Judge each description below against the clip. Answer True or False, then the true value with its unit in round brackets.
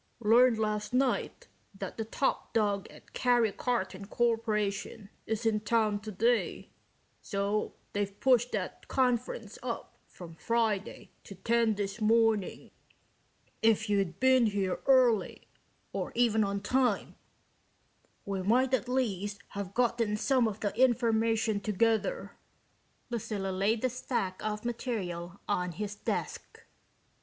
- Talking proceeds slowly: True (125 wpm)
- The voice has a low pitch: False (220 Hz)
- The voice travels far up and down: False (2.8 semitones)